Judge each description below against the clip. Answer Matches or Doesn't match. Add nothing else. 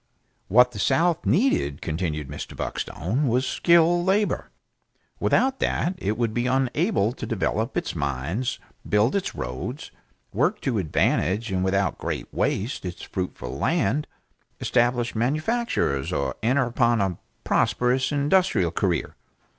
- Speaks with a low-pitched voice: Matches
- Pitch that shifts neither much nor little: Doesn't match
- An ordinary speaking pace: Doesn't match